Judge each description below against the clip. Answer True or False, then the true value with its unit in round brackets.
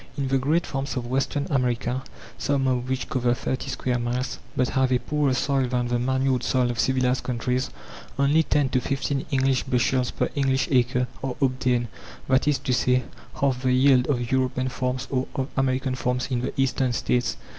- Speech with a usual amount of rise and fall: False (1.3 semitones)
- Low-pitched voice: True (130 Hz)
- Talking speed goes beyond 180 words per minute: True (190 wpm)